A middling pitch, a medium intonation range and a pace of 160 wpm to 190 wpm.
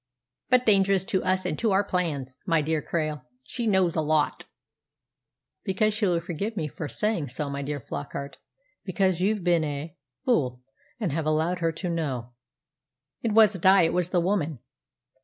Yes: medium, 170 Hz; average, 4.4 semitones; average, 170 wpm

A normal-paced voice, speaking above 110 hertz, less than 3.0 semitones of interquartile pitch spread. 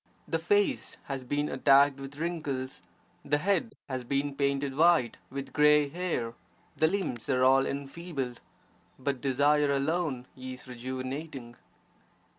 No: slow, 125 wpm; medium, 140 Hz; narrow, 2.5 semitones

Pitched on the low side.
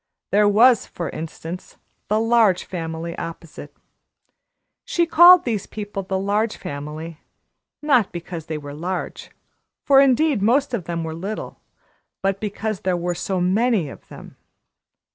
No: high, 195 Hz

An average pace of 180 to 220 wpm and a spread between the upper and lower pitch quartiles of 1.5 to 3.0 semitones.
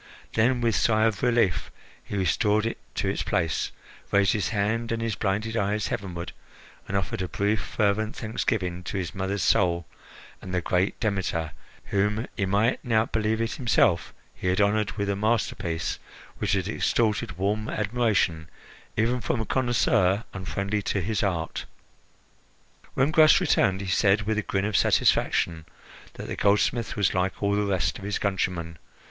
No: average, 165 wpm; average, 2.7 semitones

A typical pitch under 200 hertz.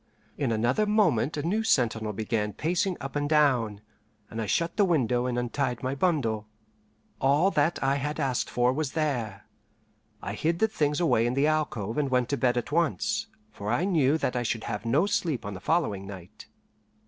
Yes: low, 135 Hz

